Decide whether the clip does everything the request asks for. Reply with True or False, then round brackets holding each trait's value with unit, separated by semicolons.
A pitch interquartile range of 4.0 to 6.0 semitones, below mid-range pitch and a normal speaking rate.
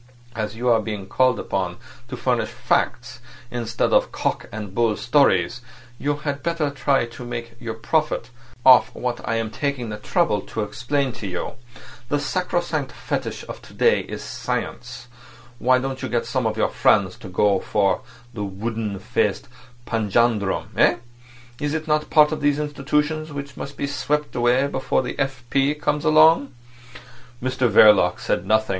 True (4.8 semitones; 125 Hz; 165 wpm)